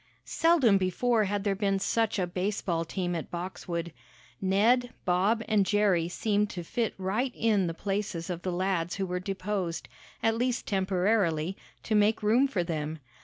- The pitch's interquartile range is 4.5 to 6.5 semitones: No, average, 3.3 semitones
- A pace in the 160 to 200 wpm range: Yes, average, 165 wpm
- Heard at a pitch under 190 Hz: No, high, 195 Hz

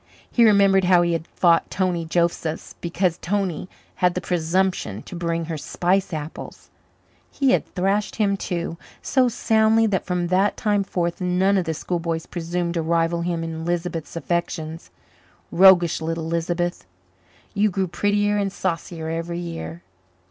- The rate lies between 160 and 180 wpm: No, average, 150 wpm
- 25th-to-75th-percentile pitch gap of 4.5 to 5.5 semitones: No, narrow, 2.5 semitones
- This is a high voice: No, medium, 175 Hz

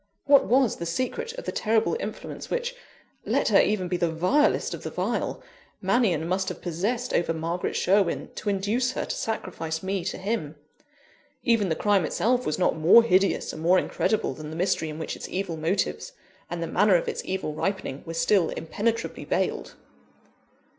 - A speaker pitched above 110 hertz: Yes, high, 190 Hz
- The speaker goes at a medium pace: Yes, average, 180 wpm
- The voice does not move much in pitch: No, average, 5.3 semitones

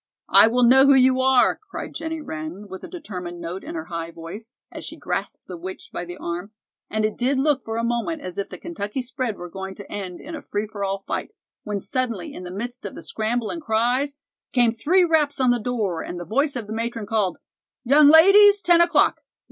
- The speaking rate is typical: No, fast, 230 wpm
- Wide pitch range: Yes, wide, 6.1 semitones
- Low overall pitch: No, high, 230 Hz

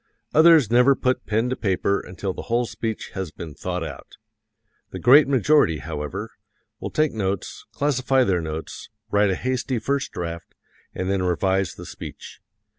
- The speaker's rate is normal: Yes, average, 160 wpm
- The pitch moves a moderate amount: No, wide, 6.0 semitones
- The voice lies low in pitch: Yes, low, 105 Hz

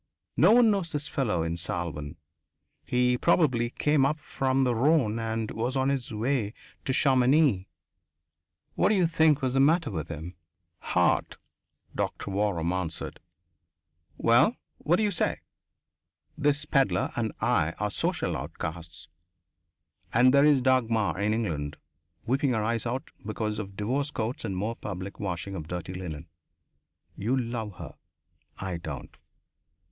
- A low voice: Yes, low, 115 Hz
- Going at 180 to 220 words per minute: No, average, 140 wpm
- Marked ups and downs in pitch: Yes, wide, 6.3 semitones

